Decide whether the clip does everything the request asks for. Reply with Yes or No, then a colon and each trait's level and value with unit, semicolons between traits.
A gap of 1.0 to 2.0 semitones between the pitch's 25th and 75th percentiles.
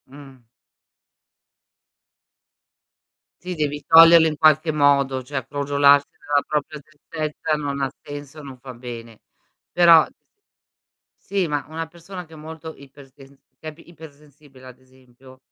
No: narrow, 2.6 semitones